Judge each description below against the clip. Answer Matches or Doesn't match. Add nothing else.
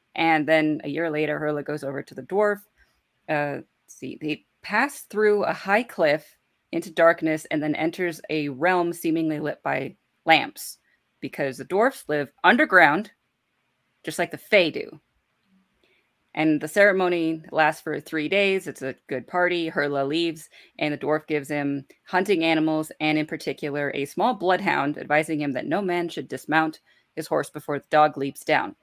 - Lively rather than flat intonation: Doesn't match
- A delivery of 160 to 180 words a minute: Matches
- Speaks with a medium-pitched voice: Matches